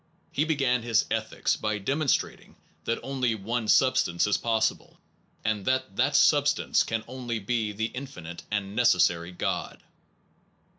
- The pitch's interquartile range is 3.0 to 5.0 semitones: Yes, average, 4.0 semitones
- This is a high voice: No, low, 115 Hz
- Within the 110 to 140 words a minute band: Yes, slow, 135 wpm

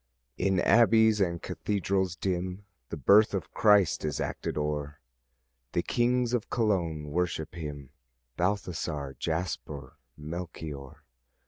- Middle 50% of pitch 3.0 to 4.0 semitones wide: No, average, 5.1 semitones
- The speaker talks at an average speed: No, slow, 110 wpm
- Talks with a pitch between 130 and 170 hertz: No, very low, 90 Hz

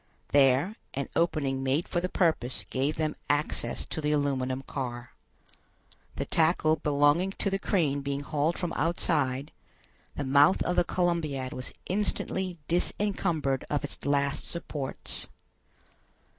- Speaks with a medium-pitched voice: Yes, medium, 150 Hz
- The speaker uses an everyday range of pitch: Yes, average, 3.8 semitones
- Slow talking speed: Yes, slow, 130 wpm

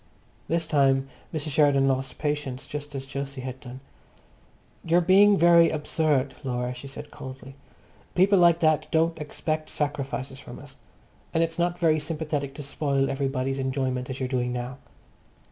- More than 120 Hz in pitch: Yes, medium, 140 Hz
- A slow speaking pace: No, average, 160 wpm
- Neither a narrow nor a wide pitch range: Yes, average, 3.1 semitones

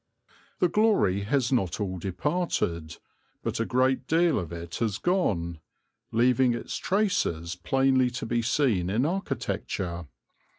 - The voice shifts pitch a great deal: Yes, wide, 8.1 semitones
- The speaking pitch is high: No, low, 120 Hz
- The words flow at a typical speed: No, slow, 130 wpm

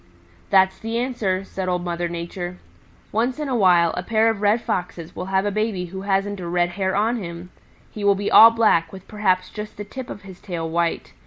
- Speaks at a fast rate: Yes, fast, 220 wpm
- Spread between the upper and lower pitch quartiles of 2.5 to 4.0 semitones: Yes, average, 3.2 semitones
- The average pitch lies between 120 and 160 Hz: No, high, 190 Hz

